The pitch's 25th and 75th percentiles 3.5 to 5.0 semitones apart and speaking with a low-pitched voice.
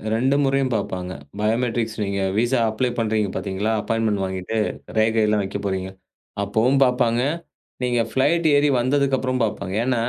Yes: average, 4.0 semitones; low, 115 Hz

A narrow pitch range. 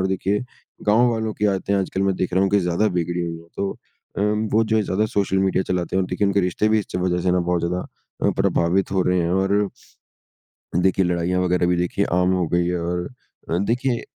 Yes: narrow, 2.3 semitones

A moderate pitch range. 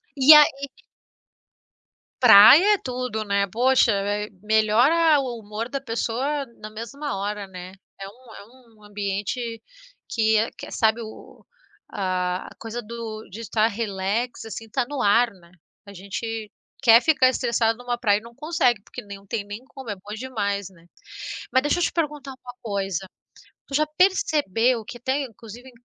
Yes: average, 3.9 semitones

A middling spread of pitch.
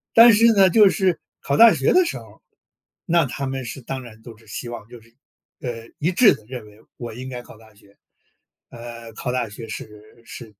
No: wide, 6.6 semitones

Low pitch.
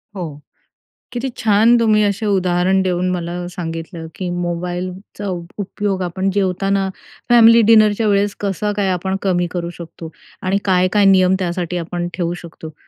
No: medium, 185 Hz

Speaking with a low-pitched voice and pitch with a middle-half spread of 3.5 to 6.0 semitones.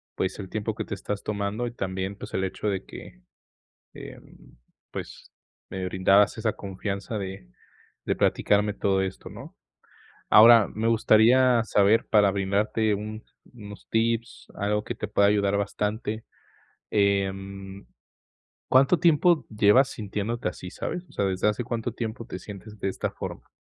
No: low, 105 Hz; narrow, 2.4 semitones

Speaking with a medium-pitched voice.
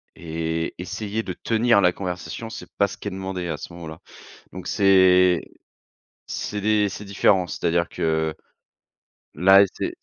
No: very low, 90 Hz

